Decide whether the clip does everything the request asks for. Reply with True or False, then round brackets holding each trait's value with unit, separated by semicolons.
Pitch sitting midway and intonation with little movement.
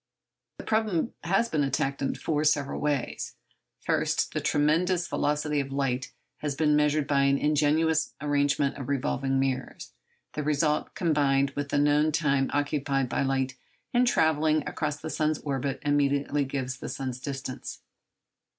True (145 Hz; 1.9 semitones)